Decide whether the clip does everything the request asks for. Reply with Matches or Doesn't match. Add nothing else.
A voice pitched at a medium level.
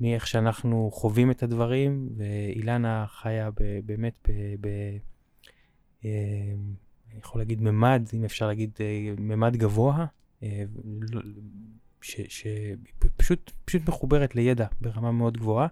Doesn't match